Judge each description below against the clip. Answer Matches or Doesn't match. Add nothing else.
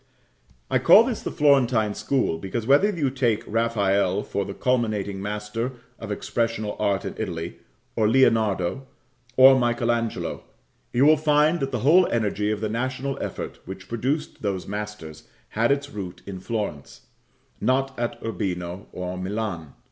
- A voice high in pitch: Doesn't match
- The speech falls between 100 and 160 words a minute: Matches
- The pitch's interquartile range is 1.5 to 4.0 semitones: Doesn't match